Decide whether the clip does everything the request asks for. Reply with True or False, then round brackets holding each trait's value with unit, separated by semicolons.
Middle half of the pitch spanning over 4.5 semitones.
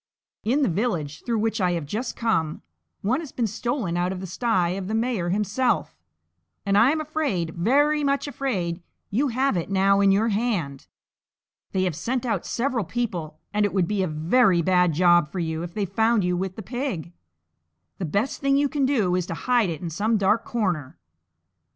True (5.6 semitones)